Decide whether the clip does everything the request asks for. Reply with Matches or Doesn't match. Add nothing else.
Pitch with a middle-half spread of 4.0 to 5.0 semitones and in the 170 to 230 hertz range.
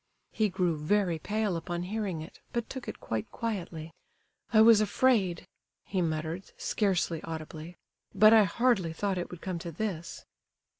Matches